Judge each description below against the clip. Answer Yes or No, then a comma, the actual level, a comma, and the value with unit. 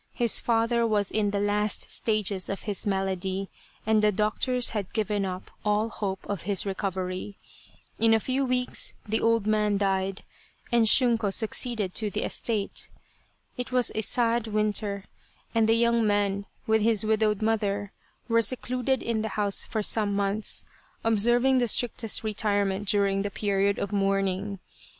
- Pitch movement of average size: No, narrow, 2.2 semitones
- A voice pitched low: No, high, 210 Hz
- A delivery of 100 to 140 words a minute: No, average, 155 wpm